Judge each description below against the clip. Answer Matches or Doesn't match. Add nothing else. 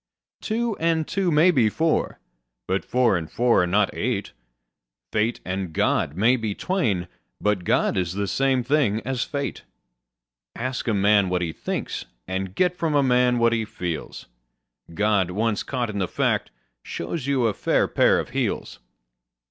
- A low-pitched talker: Matches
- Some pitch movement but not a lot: Doesn't match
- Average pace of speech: Matches